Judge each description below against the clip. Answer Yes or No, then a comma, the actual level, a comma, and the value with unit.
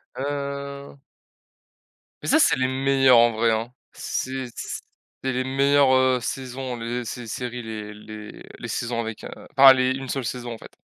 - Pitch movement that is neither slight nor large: No, narrow, 2.3 semitones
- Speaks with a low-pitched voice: Yes, low, 130 Hz